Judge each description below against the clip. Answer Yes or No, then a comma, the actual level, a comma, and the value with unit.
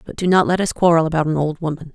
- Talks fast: Yes, fast, 310 wpm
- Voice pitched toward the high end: No, medium, 165 Hz